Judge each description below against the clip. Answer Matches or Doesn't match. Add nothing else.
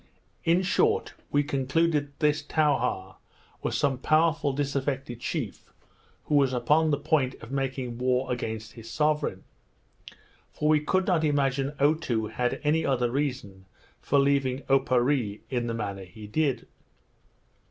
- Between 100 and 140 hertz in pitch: Matches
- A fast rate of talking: Doesn't match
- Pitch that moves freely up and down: Doesn't match